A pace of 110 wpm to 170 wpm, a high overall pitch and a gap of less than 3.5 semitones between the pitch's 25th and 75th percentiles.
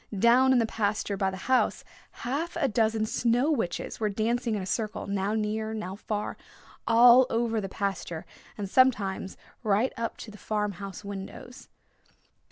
Yes: average, 165 wpm; high, 220 Hz; average, 3.0 semitones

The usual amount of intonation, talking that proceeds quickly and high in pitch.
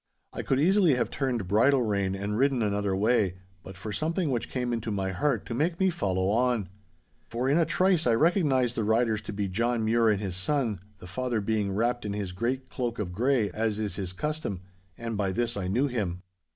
No: average, 4.5 semitones; fast, 215 wpm; low, 115 Hz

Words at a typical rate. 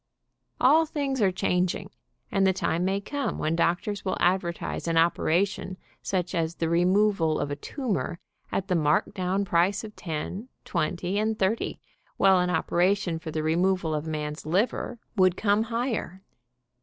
Yes: average, 160 wpm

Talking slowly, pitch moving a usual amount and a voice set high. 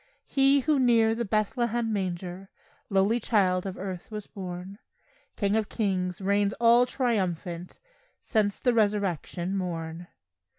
Yes: slow, 125 wpm; average, 3.7 semitones; high, 200 Hz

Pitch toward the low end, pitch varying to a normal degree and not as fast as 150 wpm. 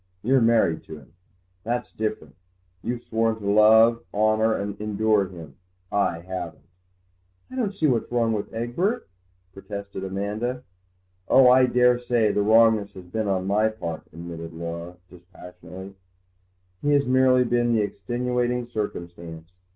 Yes: low, 110 Hz; average, 4.6 semitones; slow, 135 wpm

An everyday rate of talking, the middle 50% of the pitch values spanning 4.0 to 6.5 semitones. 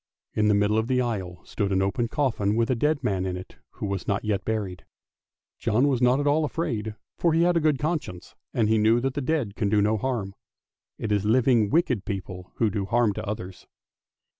No: fast, 220 wpm; average, 4.4 semitones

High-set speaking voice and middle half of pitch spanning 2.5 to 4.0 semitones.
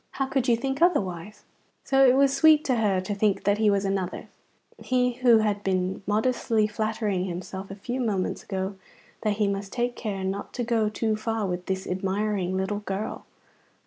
Yes: high, 210 Hz; average, 3.6 semitones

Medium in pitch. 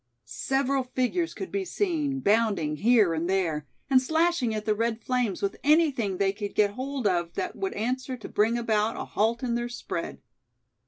No: high, 235 Hz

